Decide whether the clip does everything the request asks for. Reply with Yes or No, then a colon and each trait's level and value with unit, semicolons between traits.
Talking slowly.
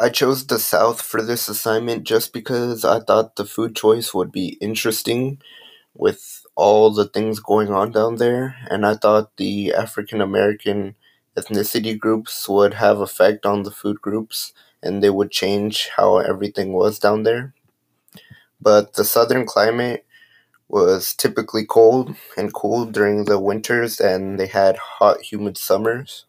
No: average, 155 wpm